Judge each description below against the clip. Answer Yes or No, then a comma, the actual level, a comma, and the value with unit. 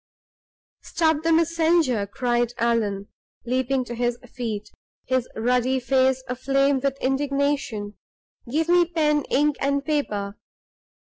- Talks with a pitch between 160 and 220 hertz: No, very high, 260 Hz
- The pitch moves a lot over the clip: No, average, 3.4 semitones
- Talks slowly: Yes, slow, 115 wpm